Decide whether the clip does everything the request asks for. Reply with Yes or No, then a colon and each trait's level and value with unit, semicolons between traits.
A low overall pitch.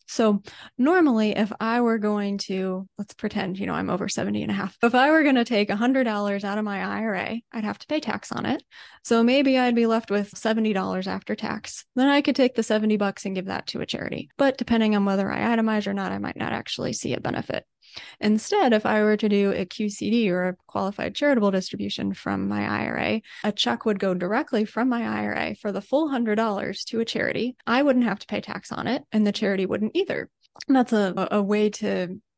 No: high, 215 Hz